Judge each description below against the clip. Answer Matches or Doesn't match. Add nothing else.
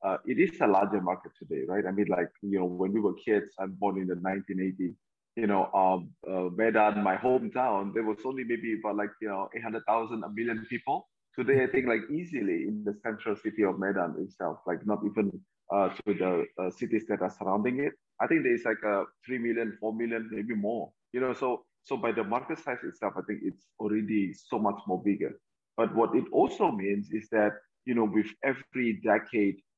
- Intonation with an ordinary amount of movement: Matches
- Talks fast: Matches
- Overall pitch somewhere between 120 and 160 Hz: Doesn't match